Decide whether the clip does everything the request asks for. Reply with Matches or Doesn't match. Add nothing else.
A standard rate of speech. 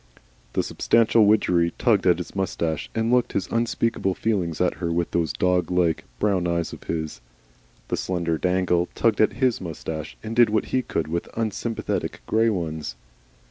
Matches